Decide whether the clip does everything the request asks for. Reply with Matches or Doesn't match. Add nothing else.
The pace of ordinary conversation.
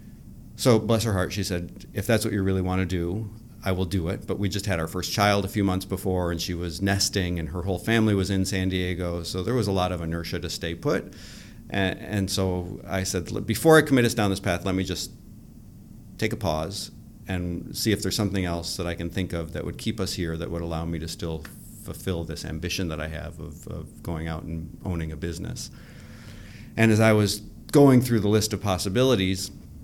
Doesn't match